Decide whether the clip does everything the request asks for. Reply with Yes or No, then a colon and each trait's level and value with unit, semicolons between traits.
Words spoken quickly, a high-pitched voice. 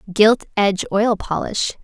No: slow, 130 wpm; high, 205 Hz